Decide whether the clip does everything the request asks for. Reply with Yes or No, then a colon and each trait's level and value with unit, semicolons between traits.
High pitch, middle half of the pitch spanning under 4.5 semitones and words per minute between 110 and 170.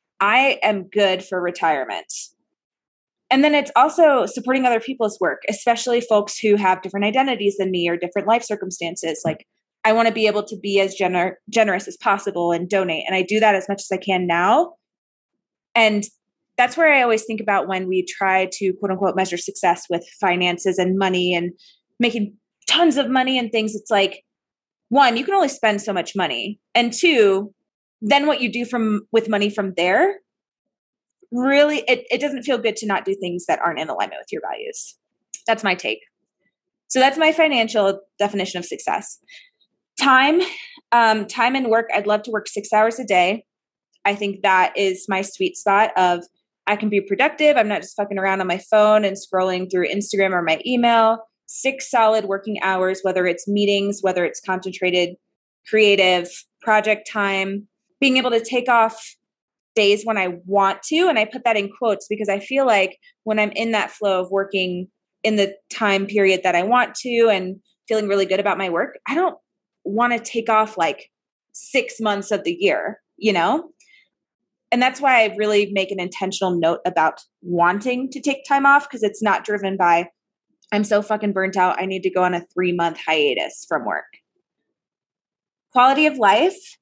No: high, 205 Hz; average, 4.0 semitones; average, 190 wpm